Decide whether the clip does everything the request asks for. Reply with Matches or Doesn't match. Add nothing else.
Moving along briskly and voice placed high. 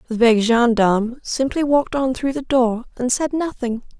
Doesn't match